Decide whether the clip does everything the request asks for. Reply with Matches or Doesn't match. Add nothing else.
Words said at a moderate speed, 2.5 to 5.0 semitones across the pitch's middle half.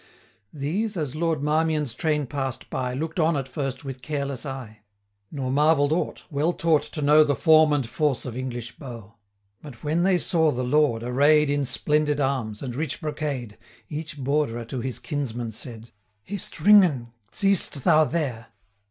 Matches